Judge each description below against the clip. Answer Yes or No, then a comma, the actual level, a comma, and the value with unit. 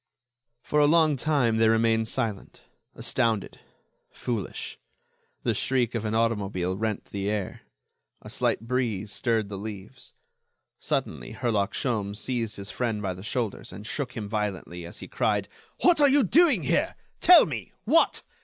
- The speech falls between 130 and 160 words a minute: Yes, average, 155 wpm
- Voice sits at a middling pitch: No, low, 110 Hz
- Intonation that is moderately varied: Yes, average, 3.8 semitones